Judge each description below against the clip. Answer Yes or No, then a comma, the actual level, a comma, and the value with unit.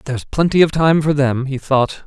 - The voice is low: No, medium, 145 Hz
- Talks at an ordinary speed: No, fast, 230 wpm